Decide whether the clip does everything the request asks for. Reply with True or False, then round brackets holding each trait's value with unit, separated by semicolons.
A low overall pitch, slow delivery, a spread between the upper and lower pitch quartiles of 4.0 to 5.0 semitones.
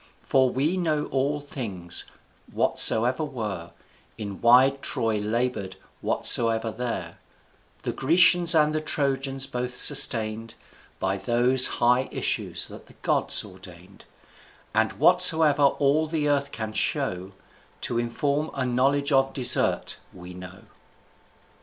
True (125 Hz; 120 wpm; 4.5 semitones)